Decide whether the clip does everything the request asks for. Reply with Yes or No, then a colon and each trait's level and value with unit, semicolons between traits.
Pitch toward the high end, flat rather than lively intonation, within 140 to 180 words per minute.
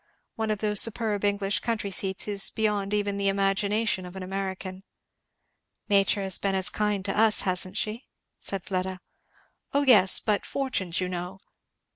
Yes: high, 200 Hz; narrow, 1.8 semitones; average, 165 wpm